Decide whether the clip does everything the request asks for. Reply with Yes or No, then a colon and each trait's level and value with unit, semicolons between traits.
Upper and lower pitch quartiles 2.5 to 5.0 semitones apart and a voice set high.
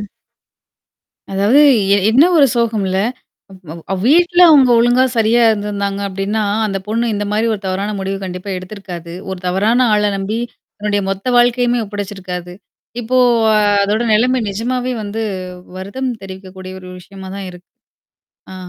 Yes: average, 3.6 semitones; high, 205 Hz